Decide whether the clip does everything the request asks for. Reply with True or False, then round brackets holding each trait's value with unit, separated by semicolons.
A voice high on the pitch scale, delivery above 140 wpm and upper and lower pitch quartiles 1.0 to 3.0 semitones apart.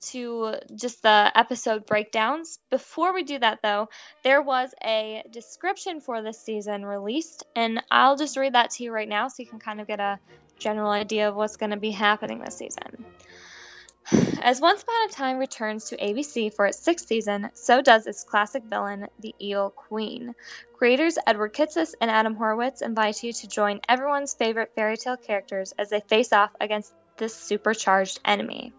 False (225 Hz; 180 wpm; 3.4 semitones)